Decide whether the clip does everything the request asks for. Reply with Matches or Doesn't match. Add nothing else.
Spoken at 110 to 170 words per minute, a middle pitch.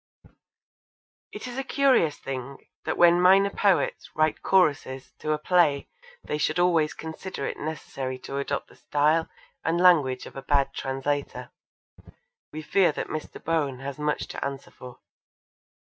Matches